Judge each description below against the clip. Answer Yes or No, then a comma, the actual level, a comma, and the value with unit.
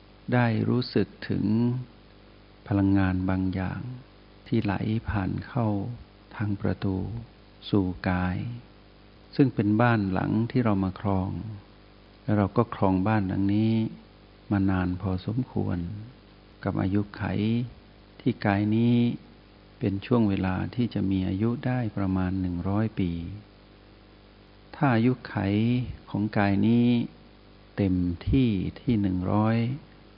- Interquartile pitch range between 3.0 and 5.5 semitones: No, narrow, 2.4 semitones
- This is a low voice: Yes, low, 105 Hz